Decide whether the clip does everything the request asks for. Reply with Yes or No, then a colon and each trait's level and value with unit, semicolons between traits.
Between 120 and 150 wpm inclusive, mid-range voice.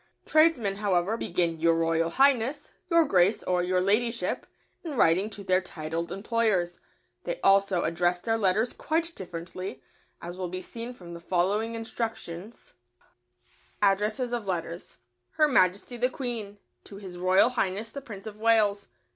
No: average, 145 wpm; high, 200 Hz